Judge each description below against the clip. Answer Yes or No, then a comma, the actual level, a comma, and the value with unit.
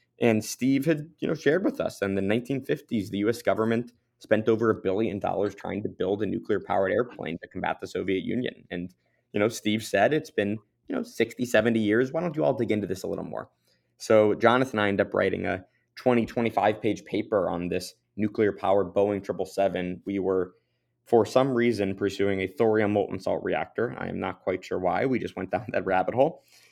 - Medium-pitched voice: No, low, 110 Hz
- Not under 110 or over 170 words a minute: No, fast, 205 wpm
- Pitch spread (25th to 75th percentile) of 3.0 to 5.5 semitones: Yes, average, 3.4 semitones